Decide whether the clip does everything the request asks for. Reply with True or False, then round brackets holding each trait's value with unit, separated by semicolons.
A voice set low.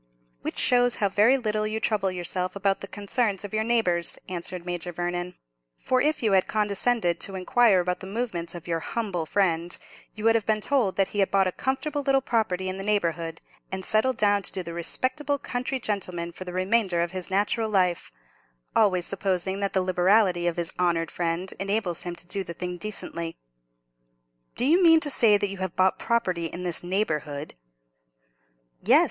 False (190 Hz)